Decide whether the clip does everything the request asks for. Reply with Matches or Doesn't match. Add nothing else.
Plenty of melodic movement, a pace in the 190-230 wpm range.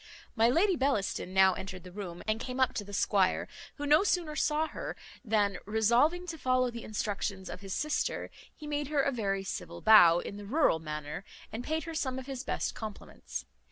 Matches